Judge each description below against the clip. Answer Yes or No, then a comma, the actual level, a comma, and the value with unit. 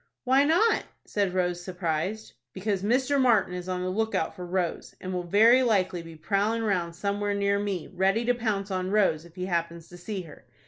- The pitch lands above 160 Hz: Yes, high, 190 Hz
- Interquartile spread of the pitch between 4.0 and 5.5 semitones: No, average, 3.4 semitones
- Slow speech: No, average, 195 wpm